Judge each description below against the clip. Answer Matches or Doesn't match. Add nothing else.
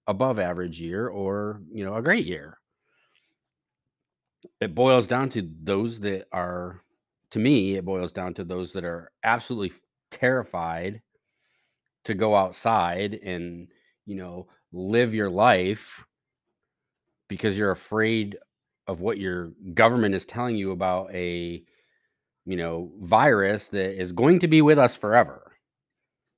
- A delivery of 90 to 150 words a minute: Matches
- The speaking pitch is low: Matches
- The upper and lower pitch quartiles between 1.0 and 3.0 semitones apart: Doesn't match